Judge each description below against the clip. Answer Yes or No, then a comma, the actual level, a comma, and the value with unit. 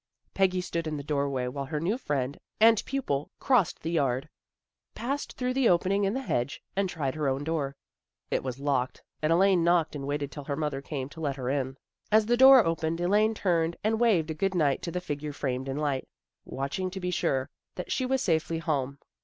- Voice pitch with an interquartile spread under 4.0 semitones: No, wide, 5.4 semitones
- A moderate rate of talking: No, fast, 215 wpm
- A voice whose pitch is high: No, medium, 160 Hz